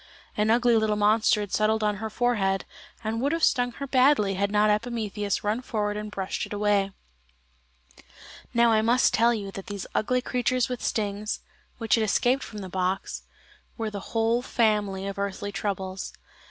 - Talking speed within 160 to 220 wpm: Yes, average, 175 wpm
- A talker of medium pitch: No, high, 215 Hz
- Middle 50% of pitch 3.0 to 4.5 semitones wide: No, narrow, 2.6 semitones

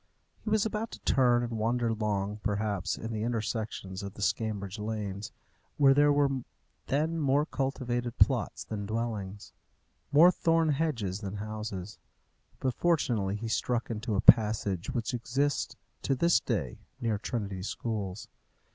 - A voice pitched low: Yes, low, 115 Hz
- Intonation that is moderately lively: Yes, average, 4.7 semitones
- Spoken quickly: No, average, 145 wpm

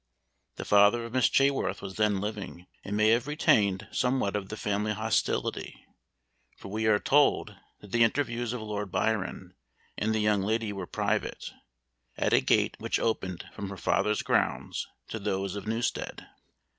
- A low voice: Yes, low, 105 Hz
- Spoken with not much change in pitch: Yes, narrow, 2.3 semitones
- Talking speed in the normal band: Yes, average, 165 wpm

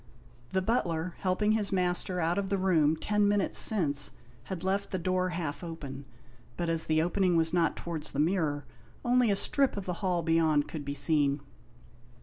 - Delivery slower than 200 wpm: Yes, average, 180 wpm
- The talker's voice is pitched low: No, medium, 175 Hz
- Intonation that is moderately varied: Yes, average, 3.3 semitones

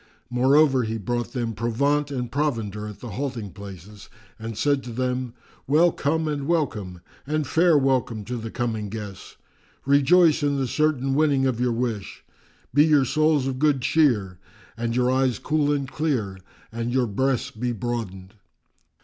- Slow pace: No, average, 160 wpm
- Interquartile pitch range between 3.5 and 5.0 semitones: Yes, average, 4.3 semitones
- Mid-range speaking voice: No, low, 125 Hz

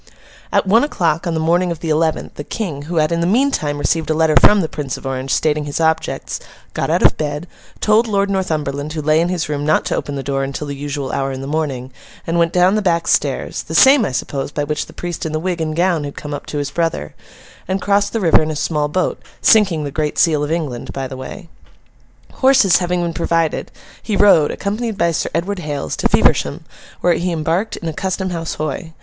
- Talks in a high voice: No, medium, 160 Hz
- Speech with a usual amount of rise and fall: Yes, average, 3.6 semitones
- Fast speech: Yes, fast, 235 wpm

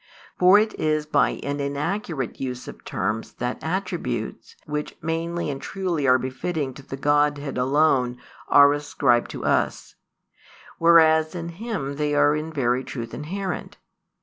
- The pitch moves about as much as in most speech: Yes, average, 3.8 semitones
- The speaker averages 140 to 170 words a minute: Yes, average, 145 wpm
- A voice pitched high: No, medium, 145 Hz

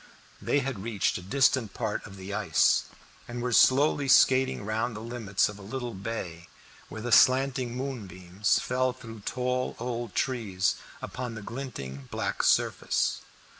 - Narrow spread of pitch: No, average, 4.1 semitones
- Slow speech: No, average, 150 wpm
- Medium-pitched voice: No, low, 115 Hz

